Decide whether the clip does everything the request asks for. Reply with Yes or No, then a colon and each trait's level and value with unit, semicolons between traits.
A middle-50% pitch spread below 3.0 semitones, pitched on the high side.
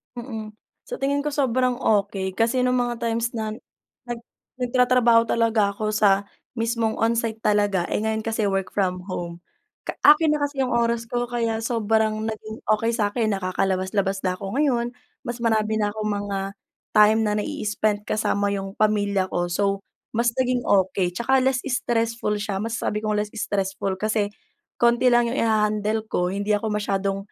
Yes: narrow, 2.6 semitones; high, 215 Hz